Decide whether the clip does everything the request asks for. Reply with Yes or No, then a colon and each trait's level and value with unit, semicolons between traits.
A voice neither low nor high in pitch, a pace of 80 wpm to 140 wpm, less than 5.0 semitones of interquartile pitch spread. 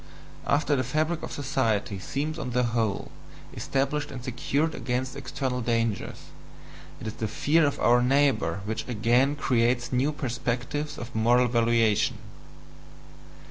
No: low, 125 Hz; slow, 135 wpm; average, 3.3 semitones